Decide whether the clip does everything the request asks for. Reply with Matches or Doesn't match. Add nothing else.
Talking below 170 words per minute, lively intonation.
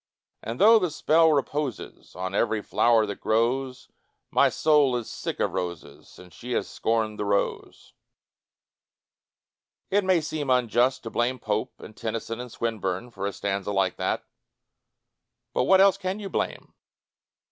Matches